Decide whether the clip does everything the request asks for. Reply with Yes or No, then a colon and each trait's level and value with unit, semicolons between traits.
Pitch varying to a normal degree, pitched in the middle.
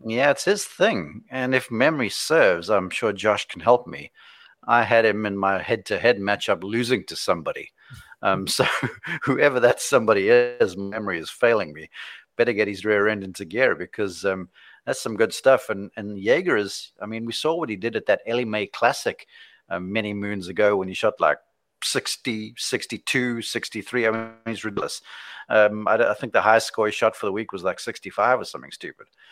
No: average, 3.0 semitones; low, 110 Hz